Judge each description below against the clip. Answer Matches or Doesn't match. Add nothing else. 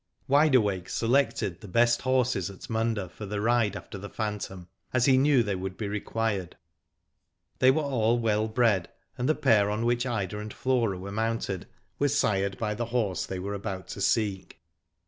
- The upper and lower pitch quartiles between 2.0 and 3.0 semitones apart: Doesn't match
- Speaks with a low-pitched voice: Matches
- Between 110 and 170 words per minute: Doesn't match